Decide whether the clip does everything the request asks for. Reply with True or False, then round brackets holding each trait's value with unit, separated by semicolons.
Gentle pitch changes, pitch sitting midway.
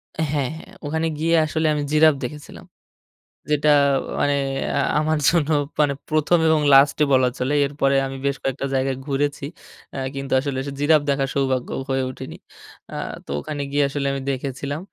True (2.0 semitones; 145 Hz)